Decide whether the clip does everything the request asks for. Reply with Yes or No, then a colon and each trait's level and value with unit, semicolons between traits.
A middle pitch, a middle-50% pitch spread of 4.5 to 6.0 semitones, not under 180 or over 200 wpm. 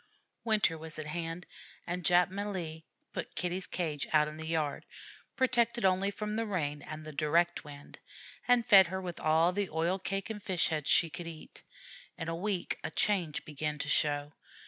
No: medium, 170 Hz; average, 3.8 semitones; average, 185 wpm